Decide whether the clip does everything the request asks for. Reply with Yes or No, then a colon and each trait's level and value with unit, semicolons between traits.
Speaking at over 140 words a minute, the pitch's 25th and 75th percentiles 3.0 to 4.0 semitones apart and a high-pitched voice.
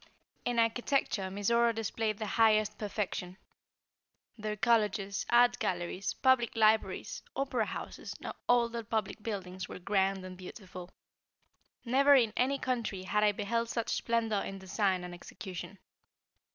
No: slow, 135 wpm; average, 3.3 semitones; high, 215 Hz